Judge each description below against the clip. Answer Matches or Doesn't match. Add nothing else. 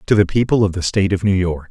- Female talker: Doesn't match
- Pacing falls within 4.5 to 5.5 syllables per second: Doesn't match